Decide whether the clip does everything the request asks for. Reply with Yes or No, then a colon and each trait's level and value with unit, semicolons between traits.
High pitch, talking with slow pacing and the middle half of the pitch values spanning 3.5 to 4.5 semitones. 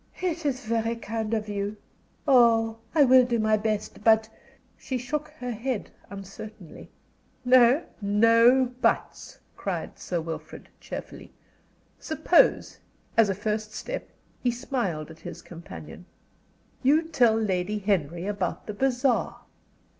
Yes: high, 225 Hz; slow, 130 wpm; average, 3.8 semitones